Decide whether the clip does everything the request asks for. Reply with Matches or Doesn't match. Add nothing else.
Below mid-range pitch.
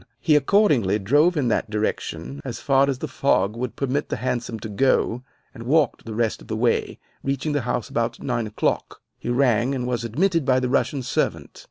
Matches